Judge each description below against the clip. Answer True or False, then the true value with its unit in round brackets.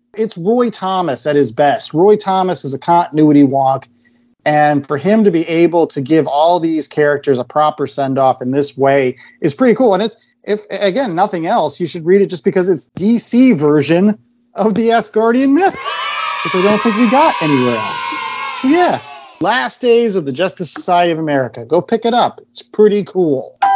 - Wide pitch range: True (7.4 semitones)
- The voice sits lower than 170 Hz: False (180 Hz)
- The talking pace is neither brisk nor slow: True (190 wpm)